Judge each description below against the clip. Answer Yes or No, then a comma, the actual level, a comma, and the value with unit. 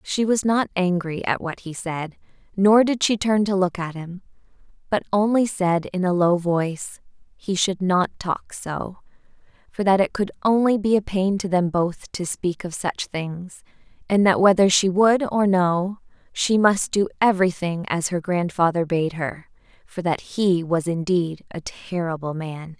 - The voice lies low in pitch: No, medium, 185 Hz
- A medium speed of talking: Yes, average, 180 wpm